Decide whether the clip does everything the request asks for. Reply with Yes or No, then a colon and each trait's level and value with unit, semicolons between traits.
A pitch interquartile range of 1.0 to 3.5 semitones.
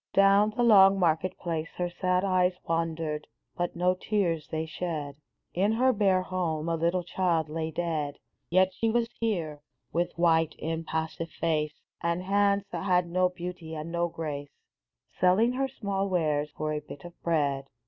Yes: average, 2.8 semitones